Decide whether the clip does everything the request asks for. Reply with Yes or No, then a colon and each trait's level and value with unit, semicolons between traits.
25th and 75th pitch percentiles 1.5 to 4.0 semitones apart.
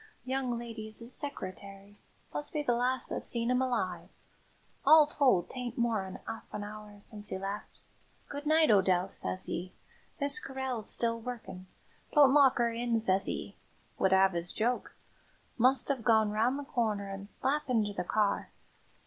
No: average, 4.4 semitones